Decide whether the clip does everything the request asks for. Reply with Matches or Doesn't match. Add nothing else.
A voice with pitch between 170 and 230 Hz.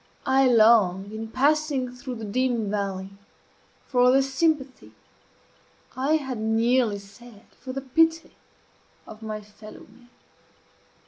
Doesn't match